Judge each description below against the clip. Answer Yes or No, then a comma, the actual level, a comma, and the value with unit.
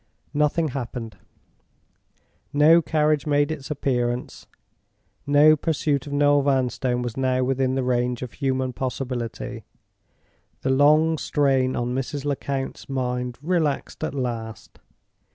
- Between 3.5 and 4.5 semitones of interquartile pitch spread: No, narrow, 2.6 semitones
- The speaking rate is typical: No, slow, 115 wpm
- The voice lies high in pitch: No, low, 135 Hz